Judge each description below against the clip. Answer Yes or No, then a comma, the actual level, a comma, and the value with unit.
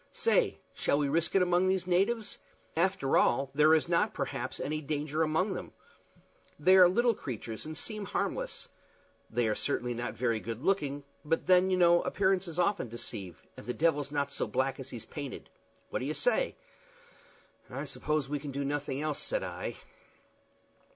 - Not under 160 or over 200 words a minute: Yes, average, 175 wpm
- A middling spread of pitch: Yes, average, 5.0 semitones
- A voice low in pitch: No, medium, 155 Hz